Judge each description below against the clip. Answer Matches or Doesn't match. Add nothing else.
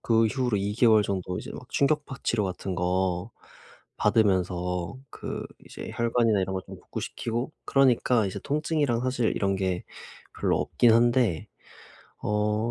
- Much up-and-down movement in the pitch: Doesn't match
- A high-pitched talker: Doesn't match